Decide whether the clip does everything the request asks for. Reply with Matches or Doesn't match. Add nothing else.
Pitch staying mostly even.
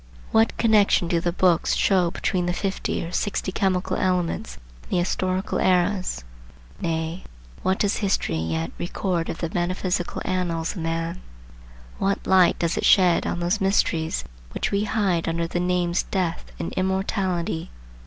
Matches